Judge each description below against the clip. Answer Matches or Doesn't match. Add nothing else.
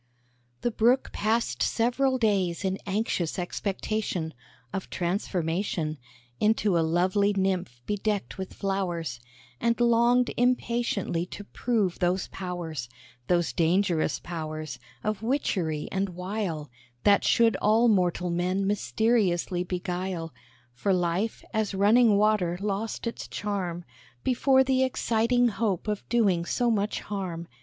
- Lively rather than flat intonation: Doesn't match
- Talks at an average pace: Doesn't match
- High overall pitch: Matches